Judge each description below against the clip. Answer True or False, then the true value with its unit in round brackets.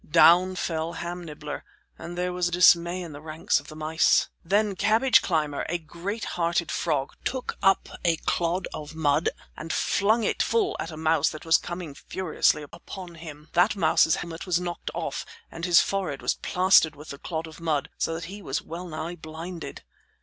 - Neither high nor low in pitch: True (170 Hz)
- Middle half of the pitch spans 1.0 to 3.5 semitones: True (2.4 semitones)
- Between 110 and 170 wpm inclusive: False (185 wpm)